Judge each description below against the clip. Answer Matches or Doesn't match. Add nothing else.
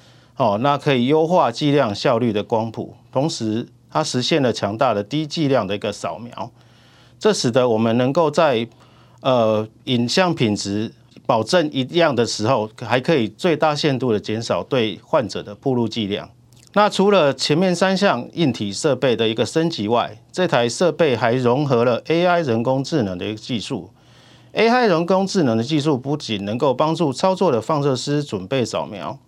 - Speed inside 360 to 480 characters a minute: Doesn't match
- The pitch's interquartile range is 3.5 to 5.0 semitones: Doesn't match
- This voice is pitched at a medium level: Doesn't match